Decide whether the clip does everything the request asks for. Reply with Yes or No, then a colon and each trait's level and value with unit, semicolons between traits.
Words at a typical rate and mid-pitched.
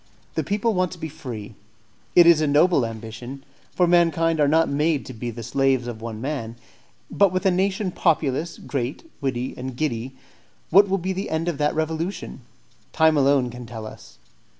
Yes: average, 185 wpm; medium, 150 Hz